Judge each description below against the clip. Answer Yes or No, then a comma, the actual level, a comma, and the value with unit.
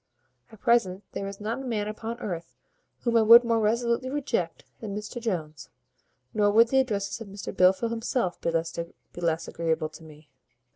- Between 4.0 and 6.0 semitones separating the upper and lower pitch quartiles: Yes, average, 5.0 semitones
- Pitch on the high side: Yes, high, 210 Hz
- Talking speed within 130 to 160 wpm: No, average, 175 wpm